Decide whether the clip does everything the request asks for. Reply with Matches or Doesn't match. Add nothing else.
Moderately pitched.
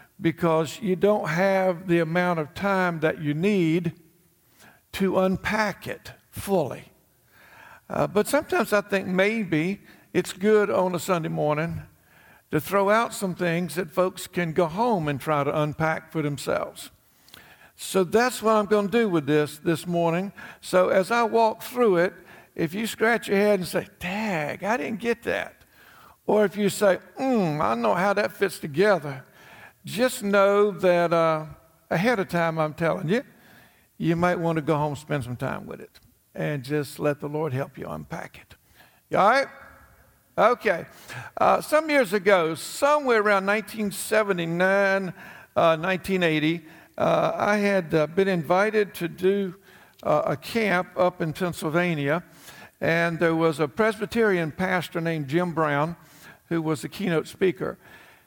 Matches